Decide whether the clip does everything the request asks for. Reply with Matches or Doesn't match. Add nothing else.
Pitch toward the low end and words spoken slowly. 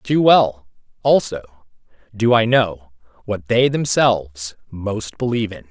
Matches